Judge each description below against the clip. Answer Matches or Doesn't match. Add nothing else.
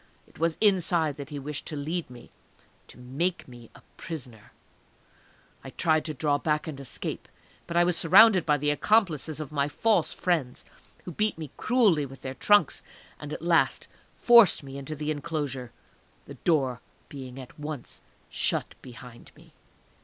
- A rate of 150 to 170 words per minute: Matches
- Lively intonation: Doesn't match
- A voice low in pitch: Doesn't match